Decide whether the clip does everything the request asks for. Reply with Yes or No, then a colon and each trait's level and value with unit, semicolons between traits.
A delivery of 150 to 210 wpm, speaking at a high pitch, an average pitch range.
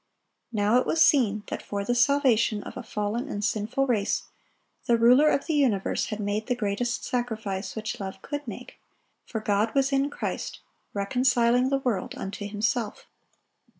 Yes: average, 165 wpm; high, 230 Hz; average, 3.7 semitones